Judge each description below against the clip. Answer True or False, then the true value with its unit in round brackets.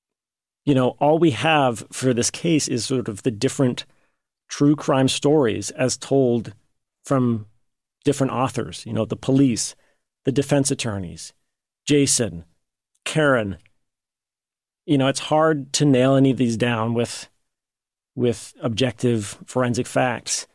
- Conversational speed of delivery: False (130 wpm)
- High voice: False (130 Hz)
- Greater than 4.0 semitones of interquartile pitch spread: False (3.0 semitones)